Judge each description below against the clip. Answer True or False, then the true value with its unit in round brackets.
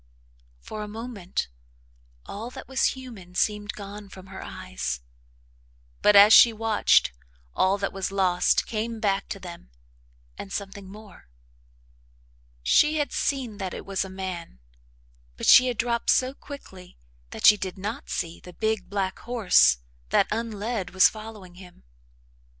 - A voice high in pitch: True (200 Hz)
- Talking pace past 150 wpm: False (145 wpm)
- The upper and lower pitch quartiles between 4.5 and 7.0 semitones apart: False (3.1 semitones)